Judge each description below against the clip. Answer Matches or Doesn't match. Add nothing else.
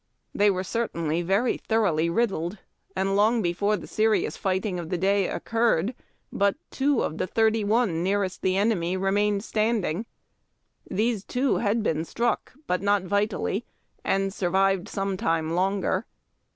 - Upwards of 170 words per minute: Doesn't match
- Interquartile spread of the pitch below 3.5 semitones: Matches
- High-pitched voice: Matches